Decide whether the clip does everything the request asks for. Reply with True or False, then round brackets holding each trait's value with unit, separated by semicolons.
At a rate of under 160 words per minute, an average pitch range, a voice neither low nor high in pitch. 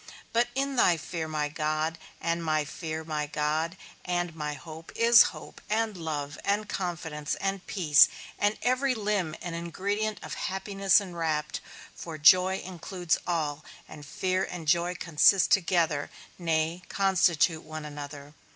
True (140 wpm; 3.7 semitones; 170 Hz)